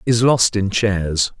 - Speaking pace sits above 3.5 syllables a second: No, 3.2 syllables/s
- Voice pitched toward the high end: No, low, 105 Hz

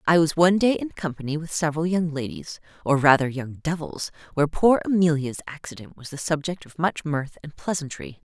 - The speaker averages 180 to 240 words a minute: Yes, average, 190 wpm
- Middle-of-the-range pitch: Yes, medium, 155 Hz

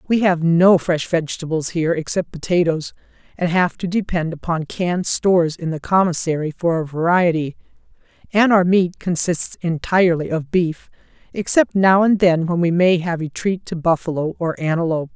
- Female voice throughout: Yes, female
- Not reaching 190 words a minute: Yes, average, 165 wpm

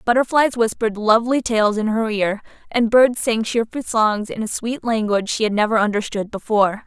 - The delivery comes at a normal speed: Yes, average, 185 wpm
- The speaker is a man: No, female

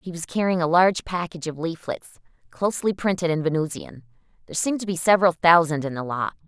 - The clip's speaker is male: No, female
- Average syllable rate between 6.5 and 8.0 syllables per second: Yes, 6.6 syllables/s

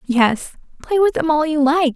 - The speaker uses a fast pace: Yes, fast, 215 wpm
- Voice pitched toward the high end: Yes, very high, 300 Hz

